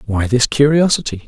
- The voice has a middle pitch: No, low, 125 Hz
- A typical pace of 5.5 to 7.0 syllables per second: No, 5.3 syllables/s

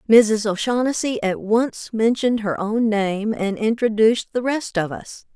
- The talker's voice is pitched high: Yes, high, 220 Hz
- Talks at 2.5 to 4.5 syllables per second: Yes, 4.4 syllables/s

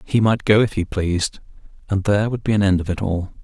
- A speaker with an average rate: No, fast, 260 wpm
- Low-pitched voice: Yes, low, 100 Hz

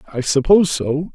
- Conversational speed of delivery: Yes, average, 155 wpm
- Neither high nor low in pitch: Yes, medium, 155 Hz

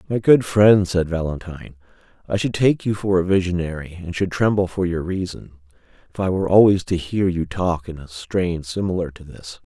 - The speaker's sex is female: No, male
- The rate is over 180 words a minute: Yes, average, 200 wpm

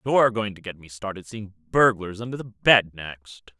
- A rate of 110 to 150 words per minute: No, average, 200 wpm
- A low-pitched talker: Yes, low, 105 Hz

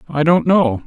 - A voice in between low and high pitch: Yes, medium, 155 Hz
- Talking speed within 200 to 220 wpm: Yes, fast, 210 wpm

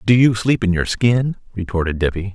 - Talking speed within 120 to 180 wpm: No, fast, 205 wpm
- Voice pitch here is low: Yes, low, 105 Hz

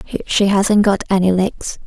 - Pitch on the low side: No, high, 200 Hz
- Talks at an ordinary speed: Yes, average, 160 wpm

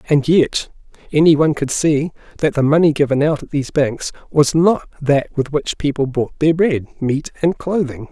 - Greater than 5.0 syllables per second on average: No, 4.9 syllables/s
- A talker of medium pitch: Yes, medium, 150 Hz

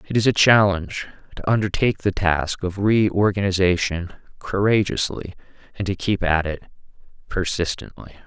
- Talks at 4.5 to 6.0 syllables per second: Yes, 5.0 syllables/s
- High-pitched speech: No, very low, 95 Hz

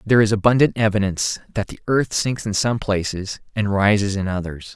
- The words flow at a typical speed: Yes, average, 190 wpm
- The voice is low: Yes, low, 105 Hz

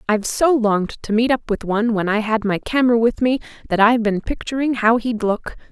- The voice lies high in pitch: Yes, high, 225 Hz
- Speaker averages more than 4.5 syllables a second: Yes, 5.9 syllables/s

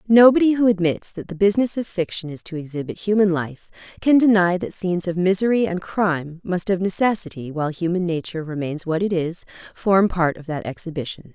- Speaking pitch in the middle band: Yes, medium, 180 Hz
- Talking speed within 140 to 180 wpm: No, average, 190 wpm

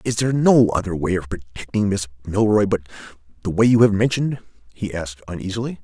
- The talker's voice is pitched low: Yes, low, 100 Hz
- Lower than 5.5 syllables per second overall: No, 6.4 syllables/s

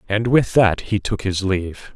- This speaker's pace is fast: Yes, fast, 215 wpm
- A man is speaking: Yes, male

